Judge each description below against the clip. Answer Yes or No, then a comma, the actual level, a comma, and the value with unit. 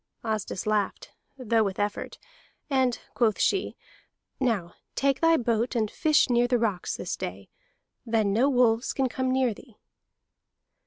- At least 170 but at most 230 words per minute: No, average, 145 wpm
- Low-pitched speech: No, high, 235 Hz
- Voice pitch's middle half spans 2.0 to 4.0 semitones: Yes, average, 3.4 semitones